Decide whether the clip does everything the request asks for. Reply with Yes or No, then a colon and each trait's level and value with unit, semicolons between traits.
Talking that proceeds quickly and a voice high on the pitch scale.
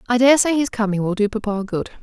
Yes: fast, 265 wpm; high, 225 Hz